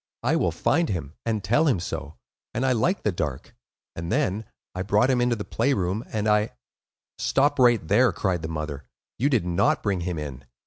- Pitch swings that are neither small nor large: No, wide, 6.6 semitones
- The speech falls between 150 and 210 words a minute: Yes, average, 195 wpm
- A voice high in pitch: No, low, 105 Hz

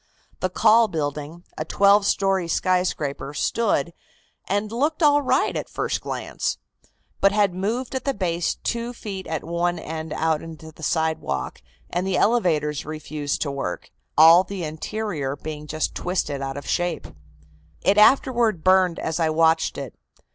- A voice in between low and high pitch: Yes, medium, 170 Hz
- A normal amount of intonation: Yes, average, 4.5 semitones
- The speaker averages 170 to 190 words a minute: No, average, 155 wpm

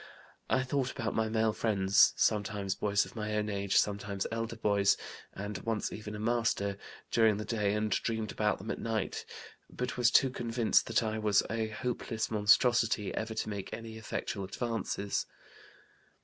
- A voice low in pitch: Yes, low, 110 Hz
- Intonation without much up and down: Yes, narrow, 1.8 semitones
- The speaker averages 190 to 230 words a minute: No, average, 165 wpm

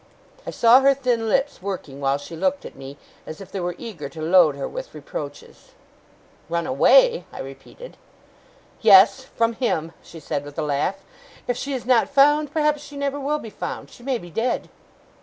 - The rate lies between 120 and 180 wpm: No, average, 190 wpm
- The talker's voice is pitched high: Yes, high, 220 Hz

